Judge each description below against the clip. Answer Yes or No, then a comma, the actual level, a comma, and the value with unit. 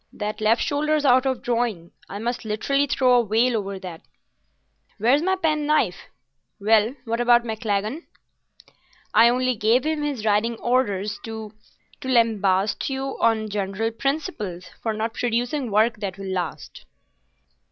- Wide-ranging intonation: No, average, 3.4 semitones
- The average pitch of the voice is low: No, high, 230 Hz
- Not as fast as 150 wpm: Yes, average, 140 wpm